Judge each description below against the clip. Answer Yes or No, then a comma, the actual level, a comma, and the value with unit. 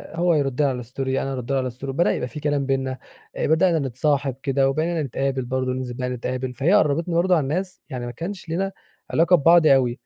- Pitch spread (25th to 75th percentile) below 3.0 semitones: No, average, 4.1 semitones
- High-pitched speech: No, low, 135 Hz